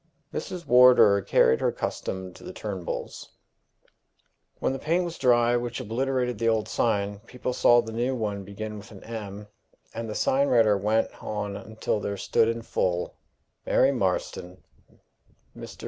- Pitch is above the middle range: No, low, 115 Hz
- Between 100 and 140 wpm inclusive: No, average, 155 wpm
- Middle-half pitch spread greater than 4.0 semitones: No, average, 3.6 semitones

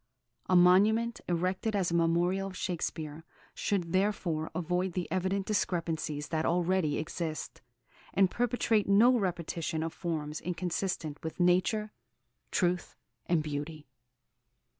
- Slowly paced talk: Yes, slow, 120 wpm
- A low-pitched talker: No, medium, 180 Hz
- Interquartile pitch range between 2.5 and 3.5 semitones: Yes, average, 3.0 semitones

